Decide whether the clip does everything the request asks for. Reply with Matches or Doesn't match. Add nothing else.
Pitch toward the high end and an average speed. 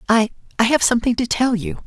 Matches